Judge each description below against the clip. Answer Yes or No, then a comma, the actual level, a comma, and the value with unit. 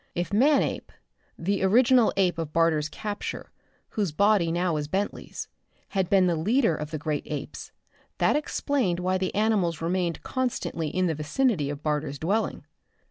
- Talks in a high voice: No, medium, 180 Hz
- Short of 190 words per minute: Yes, average, 155 wpm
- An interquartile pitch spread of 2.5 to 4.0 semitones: No, average, 4.8 semitones